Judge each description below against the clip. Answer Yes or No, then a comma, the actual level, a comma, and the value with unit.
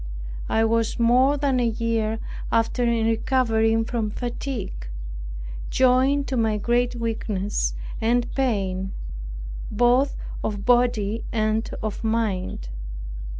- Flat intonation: Yes, narrow, 2.2 semitones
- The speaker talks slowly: Yes, slow, 110 wpm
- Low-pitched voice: No, high, 230 Hz